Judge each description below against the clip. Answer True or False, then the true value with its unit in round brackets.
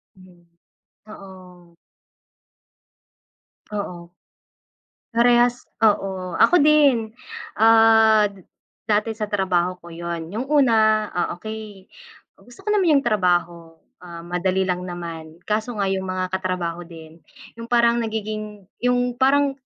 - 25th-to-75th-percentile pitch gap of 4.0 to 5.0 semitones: True (4.4 semitones)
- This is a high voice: True (205 Hz)